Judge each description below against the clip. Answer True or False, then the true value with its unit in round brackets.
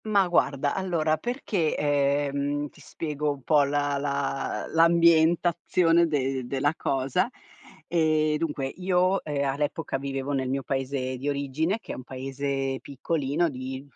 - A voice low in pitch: False (145 Hz)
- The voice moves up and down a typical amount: True (3.1 semitones)